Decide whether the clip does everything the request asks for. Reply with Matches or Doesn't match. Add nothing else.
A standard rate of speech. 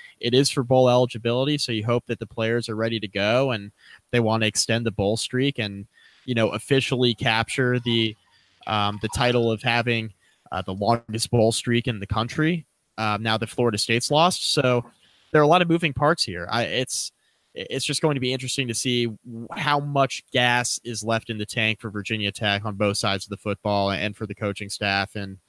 Doesn't match